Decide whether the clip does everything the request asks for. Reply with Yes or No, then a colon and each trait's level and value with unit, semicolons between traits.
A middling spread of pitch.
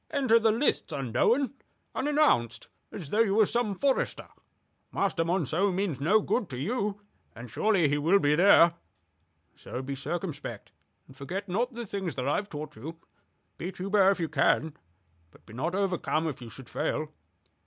No: wide, 6.1 semitones